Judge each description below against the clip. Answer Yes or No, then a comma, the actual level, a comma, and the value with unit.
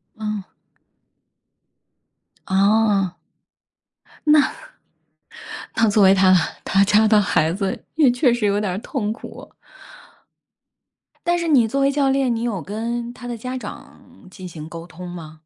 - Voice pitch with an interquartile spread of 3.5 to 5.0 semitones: Yes, average, 4.2 semitones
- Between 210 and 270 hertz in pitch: Yes, high, 215 Hz